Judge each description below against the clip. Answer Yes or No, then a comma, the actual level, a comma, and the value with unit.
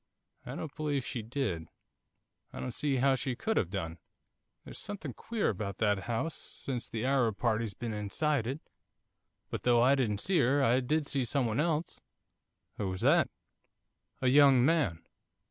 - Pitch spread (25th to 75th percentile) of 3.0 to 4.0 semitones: No, average, 4.8 semitones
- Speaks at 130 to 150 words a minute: No, average, 165 wpm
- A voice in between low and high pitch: No, low, 125 Hz